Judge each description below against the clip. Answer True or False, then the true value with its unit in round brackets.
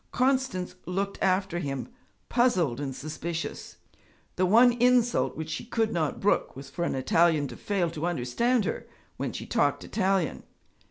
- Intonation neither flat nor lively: False (6.4 semitones)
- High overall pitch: False (180 Hz)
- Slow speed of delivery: False (155 wpm)